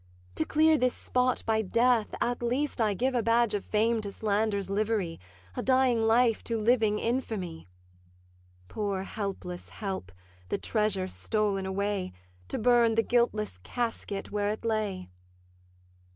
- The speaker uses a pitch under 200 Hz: No, high, 220 Hz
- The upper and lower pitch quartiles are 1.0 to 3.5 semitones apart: Yes, average, 3.0 semitones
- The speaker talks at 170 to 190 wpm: No, average, 140 wpm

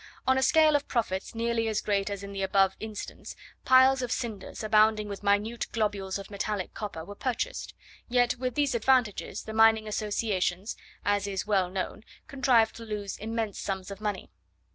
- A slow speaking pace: No, average, 175 wpm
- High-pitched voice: Yes, high, 215 Hz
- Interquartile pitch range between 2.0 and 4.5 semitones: Yes, average, 2.8 semitones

